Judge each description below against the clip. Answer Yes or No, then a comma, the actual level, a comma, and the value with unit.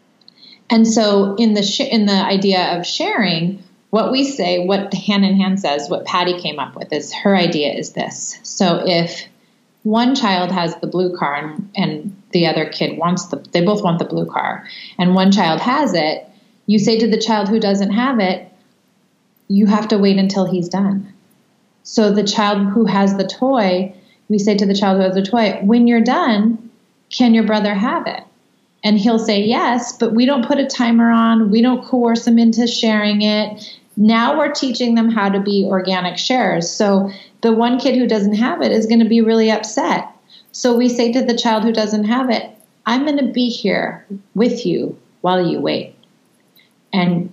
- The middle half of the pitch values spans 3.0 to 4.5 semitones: Yes, average, 3.3 semitones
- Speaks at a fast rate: No, average, 195 wpm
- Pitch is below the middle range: No, high, 210 Hz